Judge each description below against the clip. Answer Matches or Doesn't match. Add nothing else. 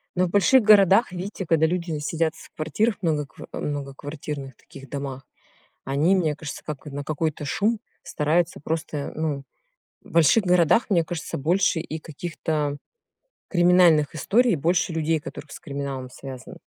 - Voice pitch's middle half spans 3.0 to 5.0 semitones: Matches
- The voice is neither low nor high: Matches